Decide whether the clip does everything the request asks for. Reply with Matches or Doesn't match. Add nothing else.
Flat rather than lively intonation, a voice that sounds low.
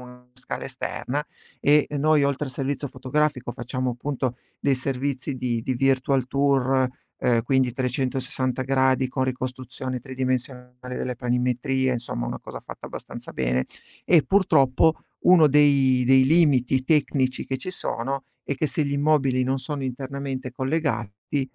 Matches